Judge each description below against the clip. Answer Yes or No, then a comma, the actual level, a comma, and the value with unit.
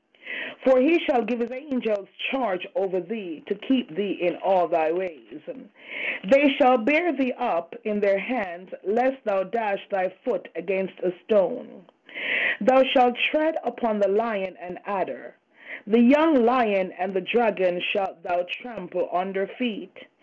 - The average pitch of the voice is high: Yes, high, 220 Hz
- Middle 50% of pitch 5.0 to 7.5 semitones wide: Yes, wide, 5.4 semitones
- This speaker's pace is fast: No, average, 150 wpm